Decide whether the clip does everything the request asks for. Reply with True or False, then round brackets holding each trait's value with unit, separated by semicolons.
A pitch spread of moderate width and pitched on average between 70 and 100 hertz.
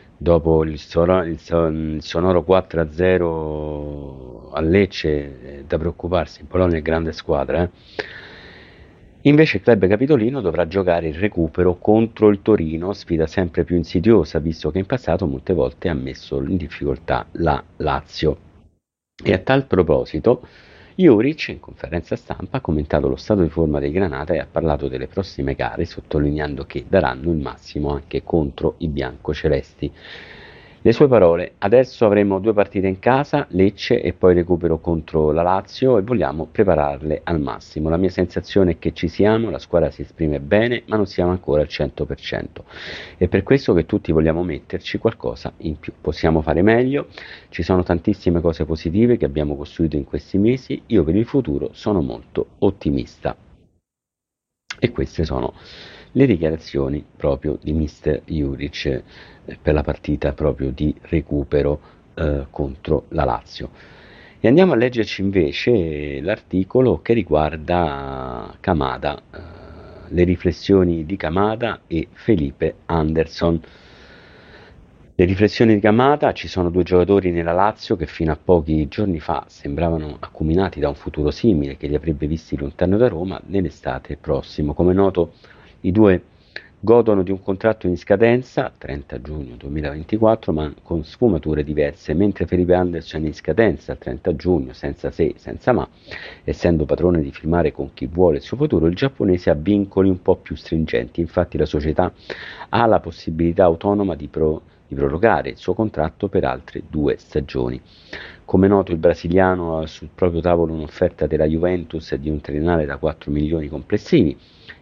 True (4.1 semitones; 85 Hz)